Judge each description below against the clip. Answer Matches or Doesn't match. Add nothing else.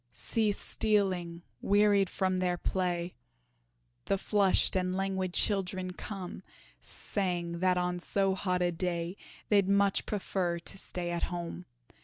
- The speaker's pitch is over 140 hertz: Matches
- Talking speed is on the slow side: Matches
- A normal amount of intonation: Doesn't match